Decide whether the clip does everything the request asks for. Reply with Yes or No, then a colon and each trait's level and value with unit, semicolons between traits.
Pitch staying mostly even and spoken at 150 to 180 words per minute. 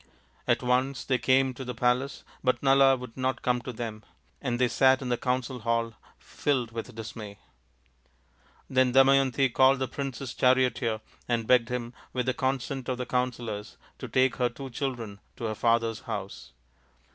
Yes: narrow, 2.0 semitones; average, 170 wpm